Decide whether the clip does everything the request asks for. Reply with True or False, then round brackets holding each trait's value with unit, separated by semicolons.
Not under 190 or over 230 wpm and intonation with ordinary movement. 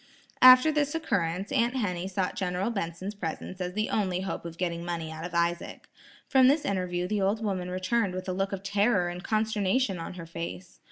True (200 wpm; 3.3 semitones)